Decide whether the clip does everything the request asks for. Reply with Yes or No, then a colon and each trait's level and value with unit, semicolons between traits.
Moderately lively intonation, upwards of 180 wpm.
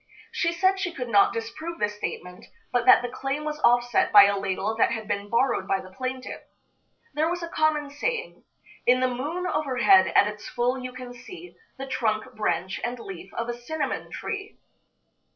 No: wide, 6.1 semitones; average, 190 wpm